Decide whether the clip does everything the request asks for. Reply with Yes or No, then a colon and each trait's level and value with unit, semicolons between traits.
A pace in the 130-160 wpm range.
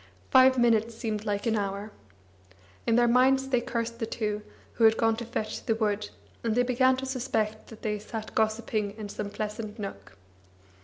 No: average, 185 wpm